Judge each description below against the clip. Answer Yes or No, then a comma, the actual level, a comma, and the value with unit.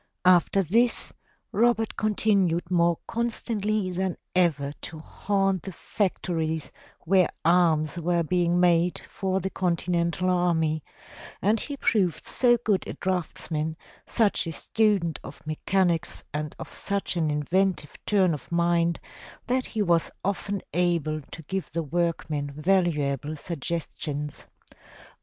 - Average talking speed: No, slow, 125 wpm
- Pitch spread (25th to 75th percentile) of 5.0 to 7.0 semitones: No, average, 3.3 semitones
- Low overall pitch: No, medium, 175 Hz